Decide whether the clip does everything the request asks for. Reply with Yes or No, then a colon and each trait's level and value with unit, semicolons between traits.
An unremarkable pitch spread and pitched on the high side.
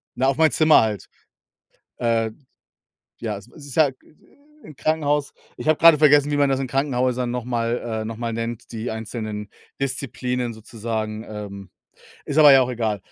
No: average, 4.0 semitones; low, 120 Hz